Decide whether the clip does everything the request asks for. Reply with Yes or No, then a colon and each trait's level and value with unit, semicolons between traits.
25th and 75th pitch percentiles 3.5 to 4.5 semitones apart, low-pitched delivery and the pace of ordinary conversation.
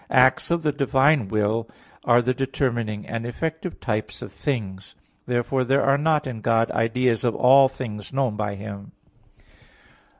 Yes: average, 3.8 semitones; low, 120 Hz; average, 160 wpm